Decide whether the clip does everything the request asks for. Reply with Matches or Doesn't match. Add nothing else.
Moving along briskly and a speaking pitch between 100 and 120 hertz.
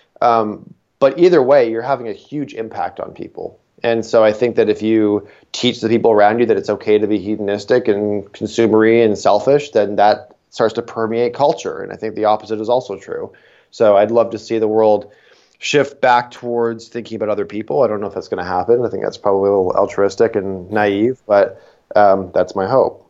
Matches